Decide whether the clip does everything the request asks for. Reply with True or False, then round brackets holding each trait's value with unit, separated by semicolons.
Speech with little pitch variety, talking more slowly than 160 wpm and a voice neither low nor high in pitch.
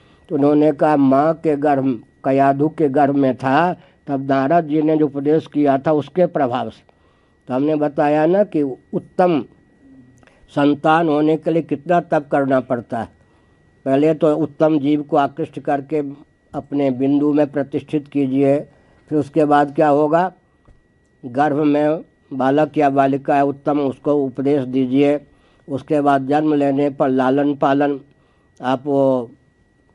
True (2.1 semitones; 145 wpm; 145 Hz)